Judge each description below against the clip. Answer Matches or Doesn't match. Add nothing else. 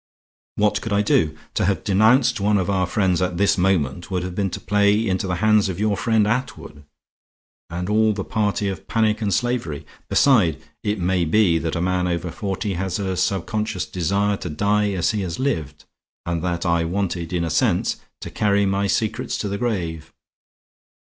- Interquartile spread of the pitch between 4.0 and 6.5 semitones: Doesn't match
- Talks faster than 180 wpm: Matches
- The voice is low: Matches